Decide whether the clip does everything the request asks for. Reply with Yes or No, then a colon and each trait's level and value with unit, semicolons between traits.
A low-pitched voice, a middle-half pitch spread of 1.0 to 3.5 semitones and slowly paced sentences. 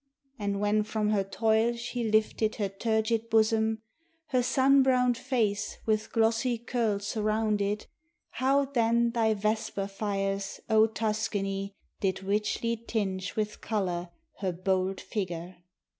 No: high, 215 Hz; narrow, 2.4 semitones; slow, 125 wpm